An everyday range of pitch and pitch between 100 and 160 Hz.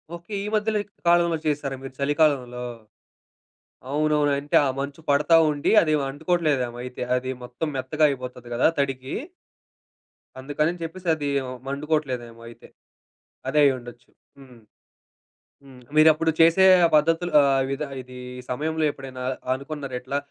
Yes: average, 3.4 semitones; medium, 140 Hz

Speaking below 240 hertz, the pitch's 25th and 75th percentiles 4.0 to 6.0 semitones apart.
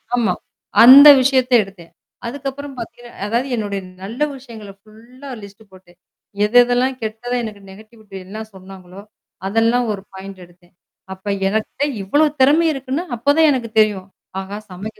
Yes: high, 220 Hz; average, 4.7 semitones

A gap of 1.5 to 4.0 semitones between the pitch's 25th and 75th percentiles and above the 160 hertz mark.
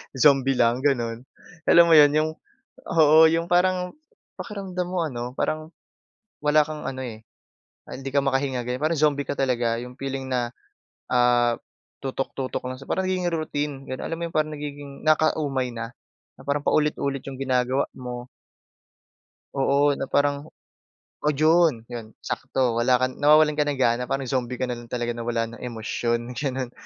No: average, 3.5 semitones; low, 135 Hz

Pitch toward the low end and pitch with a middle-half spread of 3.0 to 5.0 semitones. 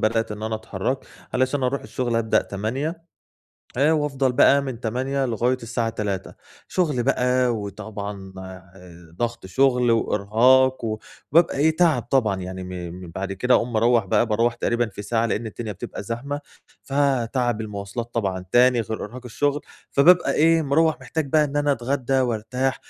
Yes: low, 120 Hz; average, 4.1 semitones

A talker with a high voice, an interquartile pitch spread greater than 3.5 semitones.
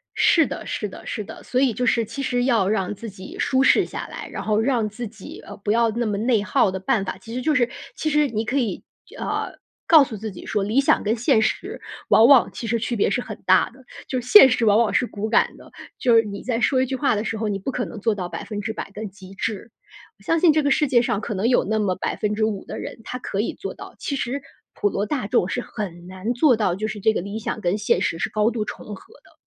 No: high, 220 Hz; average, 3.2 semitones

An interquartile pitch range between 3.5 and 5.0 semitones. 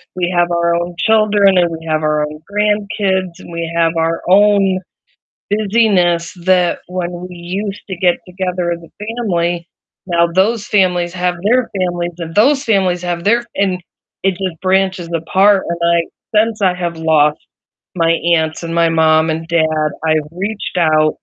No: narrow, 2.6 semitones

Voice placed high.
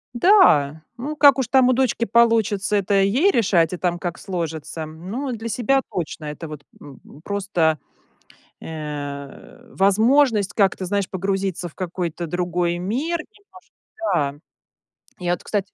Yes: high, 195 Hz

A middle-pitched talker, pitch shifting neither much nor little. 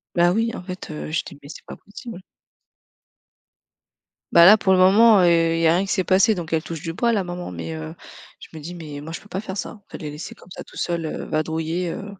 Yes: medium, 175 Hz; average, 3.4 semitones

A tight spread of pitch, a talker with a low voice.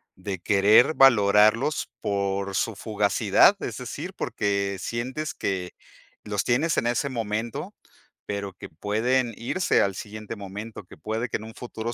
No: average, 3.0 semitones; low, 105 Hz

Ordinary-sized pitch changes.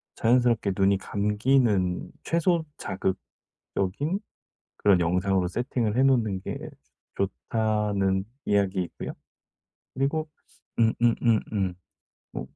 Yes: average, 4.2 semitones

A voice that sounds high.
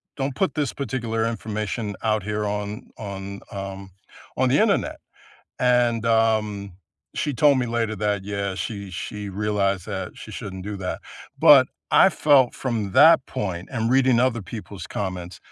No: low, 105 Hz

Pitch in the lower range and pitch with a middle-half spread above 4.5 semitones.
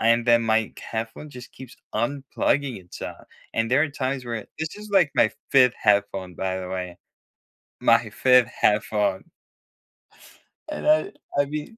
Yes: low, 120 Hz; average, 5.1 semitones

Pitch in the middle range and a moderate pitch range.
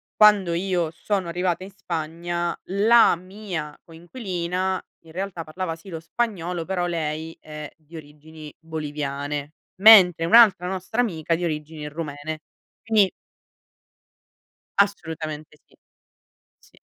Yes: medium, 170 Hz; average, 3.3 semitones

